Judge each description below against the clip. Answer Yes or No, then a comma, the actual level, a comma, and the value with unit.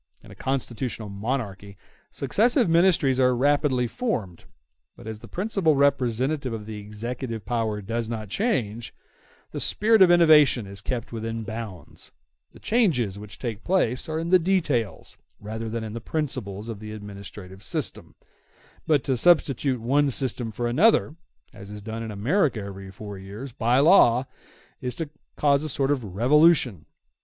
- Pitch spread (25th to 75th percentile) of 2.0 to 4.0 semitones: No, wide, 5.4 semitones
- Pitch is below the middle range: Yes, low, 120 Hz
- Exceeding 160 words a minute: No, average, 155 wpm